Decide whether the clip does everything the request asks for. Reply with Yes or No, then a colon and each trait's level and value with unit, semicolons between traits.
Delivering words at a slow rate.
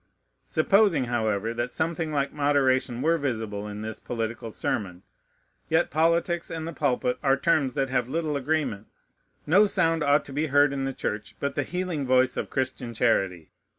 No: average, 170 wpm